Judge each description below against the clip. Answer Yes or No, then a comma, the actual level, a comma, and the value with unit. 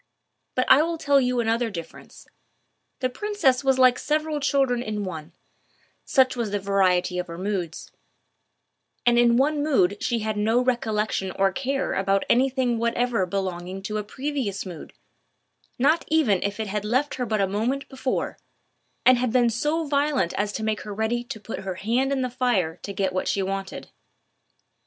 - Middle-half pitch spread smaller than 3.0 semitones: No, average, 5.0 semitones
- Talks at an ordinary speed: Yes, average, 175 wpm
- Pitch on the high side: Yes, high, 235 Hz